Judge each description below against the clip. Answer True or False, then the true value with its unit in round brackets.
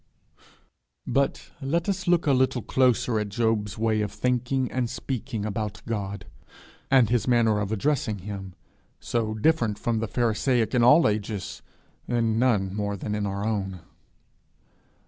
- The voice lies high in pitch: False (115 Hz)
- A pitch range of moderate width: True (3.4 semitones)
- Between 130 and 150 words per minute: True (145 wpm)